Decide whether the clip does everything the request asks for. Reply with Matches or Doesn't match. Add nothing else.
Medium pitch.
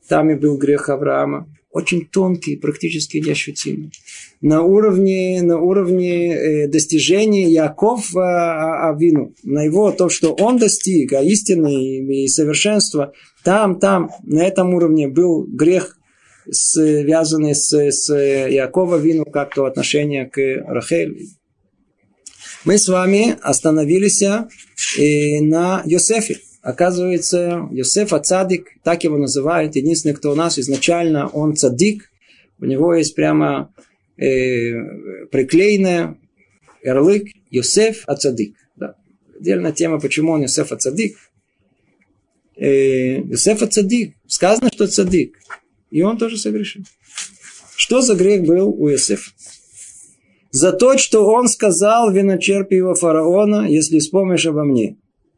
Matches